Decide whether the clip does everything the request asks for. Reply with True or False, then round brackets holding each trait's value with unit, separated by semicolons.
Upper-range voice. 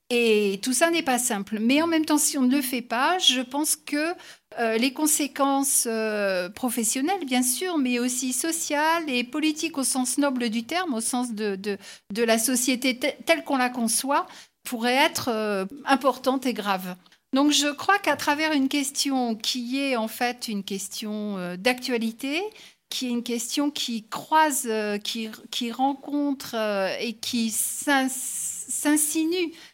True (255 Hz)